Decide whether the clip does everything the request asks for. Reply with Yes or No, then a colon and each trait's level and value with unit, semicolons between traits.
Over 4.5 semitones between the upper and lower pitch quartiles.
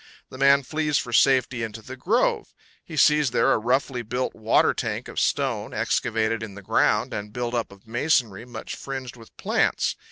No: average, 3.6 semitones